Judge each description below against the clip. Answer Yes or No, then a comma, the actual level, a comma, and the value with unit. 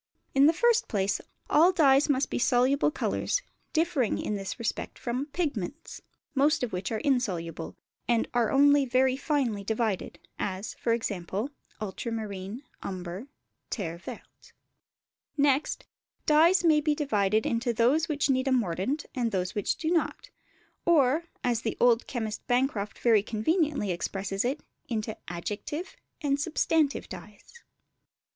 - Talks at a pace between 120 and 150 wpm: Yes, slow, 135 wpm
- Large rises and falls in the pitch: Yes, wide, 5.7 semitones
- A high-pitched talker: Yes, high, 245 Hz